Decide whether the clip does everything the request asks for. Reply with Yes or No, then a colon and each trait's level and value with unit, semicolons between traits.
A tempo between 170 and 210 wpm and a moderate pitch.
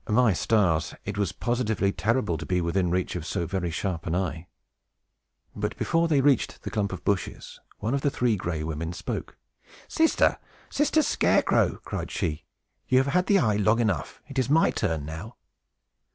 No: average, 180 wpm; low, 105 Hz